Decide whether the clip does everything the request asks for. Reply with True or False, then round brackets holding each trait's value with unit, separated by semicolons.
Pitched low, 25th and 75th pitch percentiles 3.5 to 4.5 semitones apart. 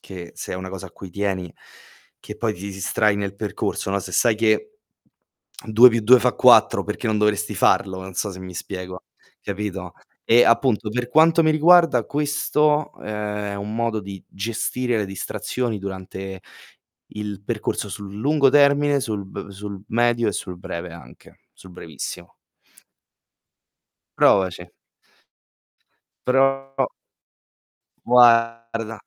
True (105 Hz; 4.2 semitones)